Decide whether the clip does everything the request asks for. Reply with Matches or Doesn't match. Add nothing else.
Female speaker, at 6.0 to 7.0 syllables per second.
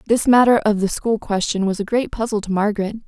Matches